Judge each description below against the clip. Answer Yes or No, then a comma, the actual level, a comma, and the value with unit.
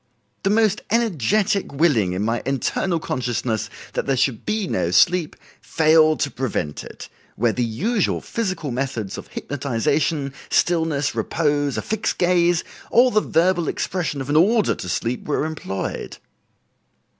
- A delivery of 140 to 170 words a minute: Yes, average, 145 wpm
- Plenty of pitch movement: Yes, wide, 6.6 semitones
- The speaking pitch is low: No, medium, 150 Hz